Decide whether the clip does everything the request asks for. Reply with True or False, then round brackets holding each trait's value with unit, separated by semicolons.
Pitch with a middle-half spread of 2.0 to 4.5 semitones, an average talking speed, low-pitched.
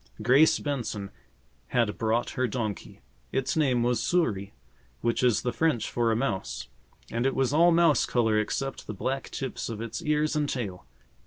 True (3.8 semitones; 170 wpm; 125 Hz)